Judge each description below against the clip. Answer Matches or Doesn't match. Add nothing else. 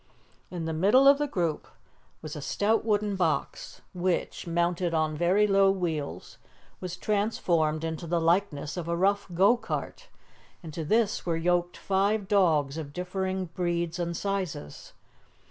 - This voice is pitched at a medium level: Matches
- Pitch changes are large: Doesn't match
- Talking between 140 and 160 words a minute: Matches